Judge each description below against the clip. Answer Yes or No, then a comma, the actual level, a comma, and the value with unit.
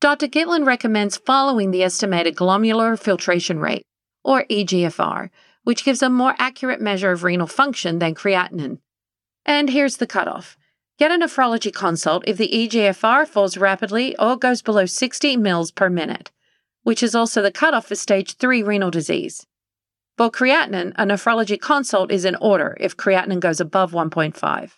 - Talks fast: No, average, 155 wpm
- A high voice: Yes, high, 210 Hz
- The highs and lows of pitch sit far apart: Yes, wide, 5.7 semitones